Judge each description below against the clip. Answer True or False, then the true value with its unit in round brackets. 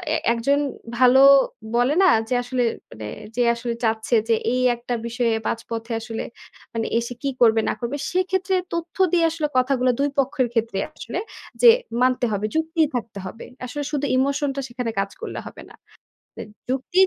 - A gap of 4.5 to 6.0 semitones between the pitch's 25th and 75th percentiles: False (3.8 semitones)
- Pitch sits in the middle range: False (250 Hz)